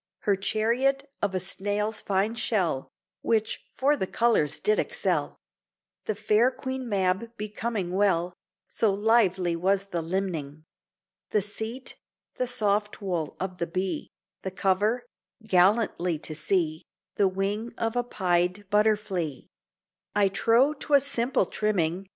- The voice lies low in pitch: No, high, 205 Hz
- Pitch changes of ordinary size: Yes, average, 3.7 semitones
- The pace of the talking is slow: Yes, slow, 130 wpm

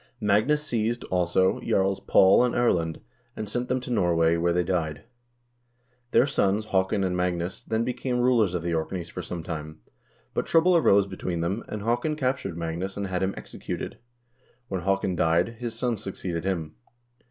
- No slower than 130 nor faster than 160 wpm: No, average, 175 wpm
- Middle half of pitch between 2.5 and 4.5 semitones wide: No, average, 5.2 semitones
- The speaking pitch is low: Yes, very low, 95 Hz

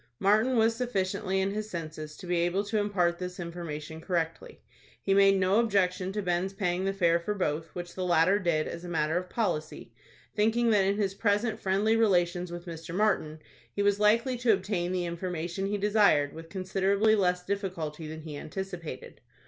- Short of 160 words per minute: No, average, 185 wpm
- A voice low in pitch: No, medium, 185 Hz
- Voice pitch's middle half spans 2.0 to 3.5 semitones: Yes, average, 3.0 semitones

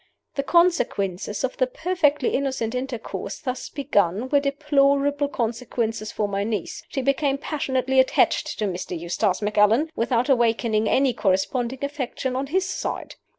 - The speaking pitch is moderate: No, very high, 255 Hz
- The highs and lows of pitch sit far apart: No, average, 4.5 semitones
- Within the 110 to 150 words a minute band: Yes, average, 140 wpm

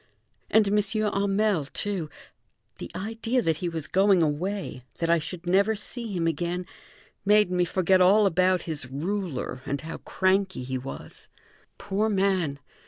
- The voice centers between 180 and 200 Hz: Yes, medium, 185 Hz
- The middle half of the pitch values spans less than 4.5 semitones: Yes, average, 3.7 semitones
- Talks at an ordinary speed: Yes, average, 150 wpm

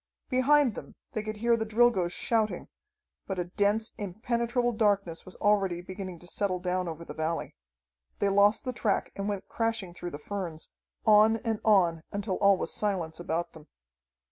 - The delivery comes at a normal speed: Yes, average, 170 wpm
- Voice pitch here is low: No, high, 200 Hz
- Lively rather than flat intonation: No, average, 3.7 semitones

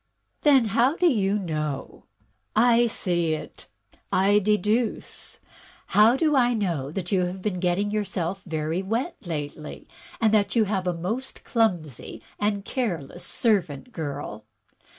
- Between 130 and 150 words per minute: Yes, average, 145 wpm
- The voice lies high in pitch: Yes, high, 195 Hz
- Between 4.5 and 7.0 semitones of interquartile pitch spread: Yes, average, 5.1 semitones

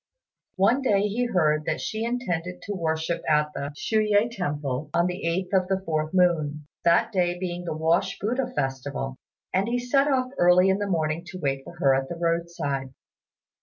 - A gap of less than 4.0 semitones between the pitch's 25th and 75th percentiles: No, average, 4.9 semitones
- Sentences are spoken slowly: No, average, 190 wpm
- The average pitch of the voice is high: No, medium, 175 Hz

